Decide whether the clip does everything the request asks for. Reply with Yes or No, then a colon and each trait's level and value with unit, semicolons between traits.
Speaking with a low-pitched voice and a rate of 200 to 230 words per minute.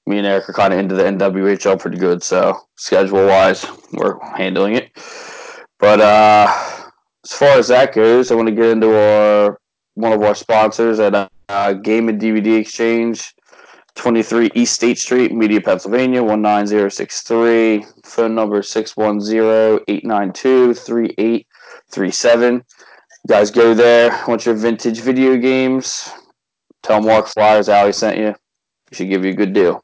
No: low, 110 Hz; average, 170 wpm